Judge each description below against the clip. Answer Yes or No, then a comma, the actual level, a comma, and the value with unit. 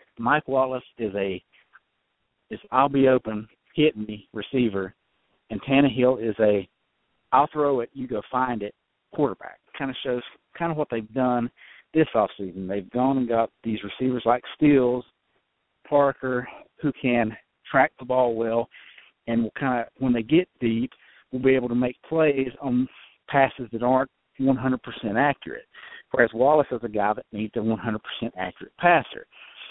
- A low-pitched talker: Yes, low, 125 Hz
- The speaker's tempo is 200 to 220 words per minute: No, average, 170 wpm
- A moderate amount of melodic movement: Yes, average, 3.0 semitones